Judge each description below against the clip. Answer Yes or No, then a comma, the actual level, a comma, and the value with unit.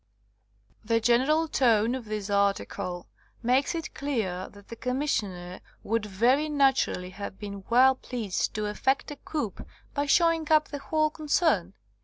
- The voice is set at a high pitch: Yes, high, 240 Hz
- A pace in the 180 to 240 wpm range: No, average, 145 wpm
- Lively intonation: Yes, wide, 6.1 semitones